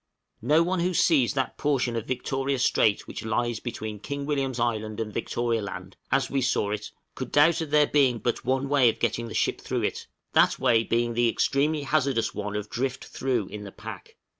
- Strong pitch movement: No, average, 3.6 semitones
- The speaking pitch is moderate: No, low, 125 Hz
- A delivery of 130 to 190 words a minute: No, fast, 205 wpm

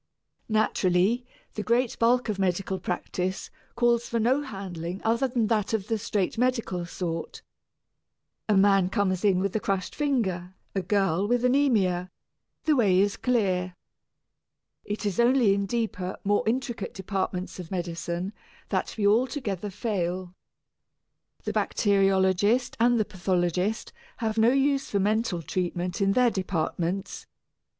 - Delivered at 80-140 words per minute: Yes, slow, 135 wpm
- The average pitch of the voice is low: No, high, 200 Hz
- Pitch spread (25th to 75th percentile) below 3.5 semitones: No, average, 4.0 semitones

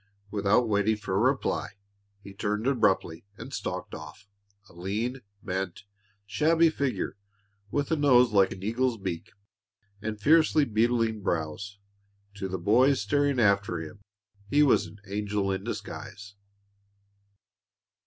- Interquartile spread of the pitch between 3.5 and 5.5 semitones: Yes, average, 4.4 semitones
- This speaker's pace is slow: Yes, slow, 130 wpm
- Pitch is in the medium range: No, low, 105 Hz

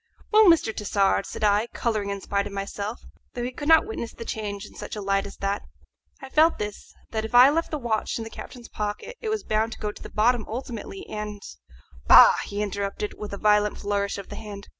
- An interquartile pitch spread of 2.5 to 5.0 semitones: Yes, average, 3.2 semitones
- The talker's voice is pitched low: No, high, 210 Hz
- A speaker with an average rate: No, fast, 230 wpm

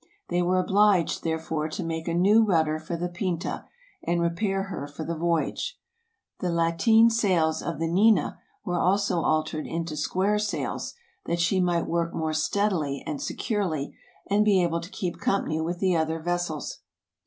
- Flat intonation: No, average, 3.3 semitones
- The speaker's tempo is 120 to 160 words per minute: No, average, 180 wpm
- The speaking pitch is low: No, medium, 170 Hz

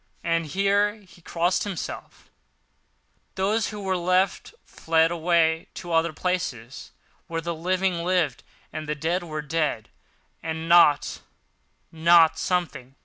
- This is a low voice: No, medium, 170 Hz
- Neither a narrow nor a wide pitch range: No, narrow, 2.3 semitones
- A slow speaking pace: Yes, slow, 120 wpm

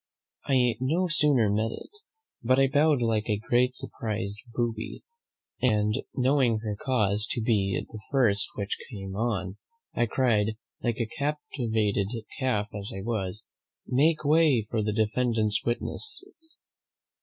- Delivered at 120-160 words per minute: Yes, slow, 135 wpm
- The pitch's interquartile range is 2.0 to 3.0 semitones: No, average, 3.7 semitones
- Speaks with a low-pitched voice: Yes, low, 115 Hz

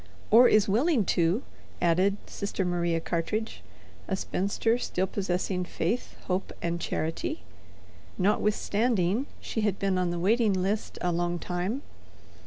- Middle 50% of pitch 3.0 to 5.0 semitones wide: Yes, average, 3.5 semitones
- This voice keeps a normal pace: No, slow, 130 wpm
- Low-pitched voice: No, high, 190 Hz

